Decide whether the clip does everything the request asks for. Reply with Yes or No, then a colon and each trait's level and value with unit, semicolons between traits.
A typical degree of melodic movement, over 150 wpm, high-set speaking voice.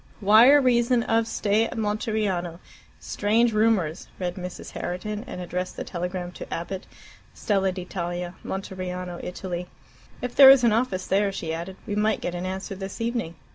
Yes: average, 3.7 semitones; average, 160 wpm; high, 195 Hz